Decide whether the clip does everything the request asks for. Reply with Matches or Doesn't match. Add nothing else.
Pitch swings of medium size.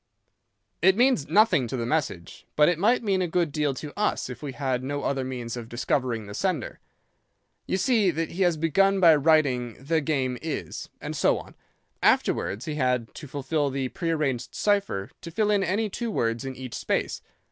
Doesn't match